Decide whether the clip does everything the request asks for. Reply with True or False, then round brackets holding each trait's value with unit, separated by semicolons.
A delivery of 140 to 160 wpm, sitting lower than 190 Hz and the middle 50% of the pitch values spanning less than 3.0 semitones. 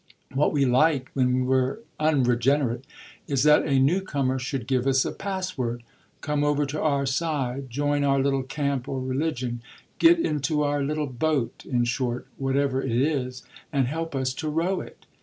False (170 wpm; 135 Hz; 2.6 semitones)